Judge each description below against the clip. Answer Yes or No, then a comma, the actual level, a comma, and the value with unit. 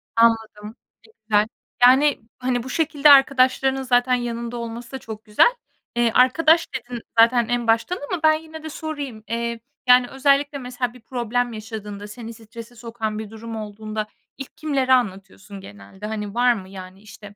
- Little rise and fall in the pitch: No, average, 3.2 semitones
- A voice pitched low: No, high, 235 Hz